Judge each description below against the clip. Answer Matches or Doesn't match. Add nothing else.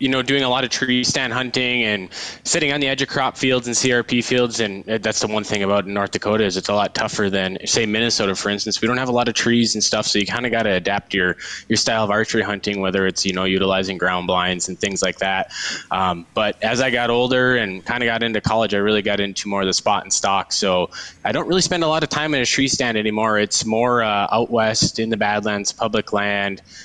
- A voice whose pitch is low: Matches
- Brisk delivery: Matches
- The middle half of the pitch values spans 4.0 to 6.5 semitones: Doesn't match